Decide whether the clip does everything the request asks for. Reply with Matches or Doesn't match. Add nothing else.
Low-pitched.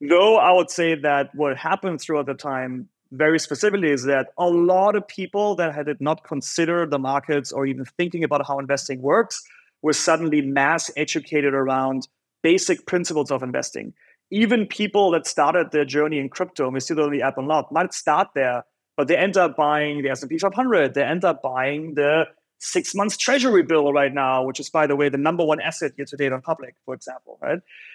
Doesn't match